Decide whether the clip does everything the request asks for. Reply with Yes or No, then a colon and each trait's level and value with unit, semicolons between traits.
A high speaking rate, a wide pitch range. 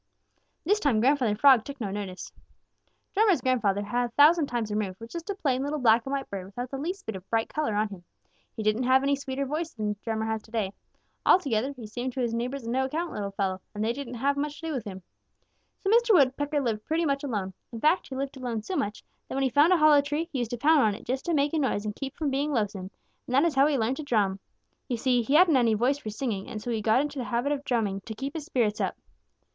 No: fast, 260 wpm; average, 4.7 semitones